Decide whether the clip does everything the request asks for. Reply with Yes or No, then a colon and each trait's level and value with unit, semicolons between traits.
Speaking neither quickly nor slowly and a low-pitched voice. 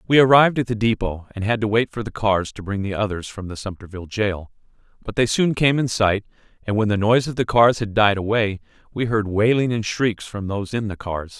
No: fast, 240 wpm; low, 110 Hz